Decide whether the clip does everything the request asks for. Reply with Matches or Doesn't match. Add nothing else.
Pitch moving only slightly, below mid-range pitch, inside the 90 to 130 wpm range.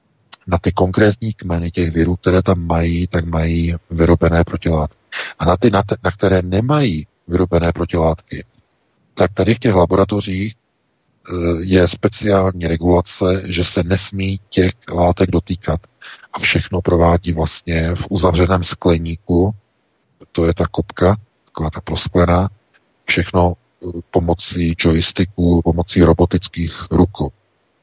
Matches